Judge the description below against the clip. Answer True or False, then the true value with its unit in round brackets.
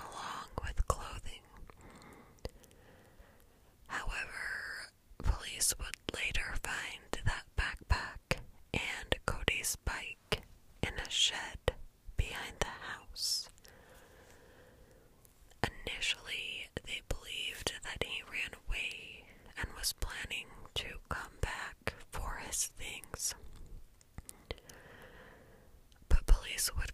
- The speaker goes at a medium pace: False (85 wpm)